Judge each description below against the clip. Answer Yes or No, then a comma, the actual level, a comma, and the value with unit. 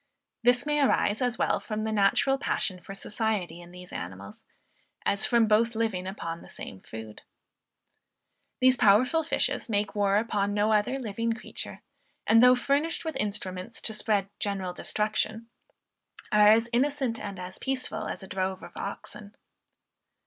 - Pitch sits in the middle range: No, high, 215 Hz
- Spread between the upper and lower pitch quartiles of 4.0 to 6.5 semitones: No, average, 3.5 semitones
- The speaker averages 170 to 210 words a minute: No, average, 155 wpm